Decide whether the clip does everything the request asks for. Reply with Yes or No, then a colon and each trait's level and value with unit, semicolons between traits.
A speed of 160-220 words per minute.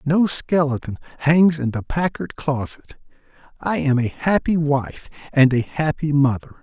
No: average, 145 wpm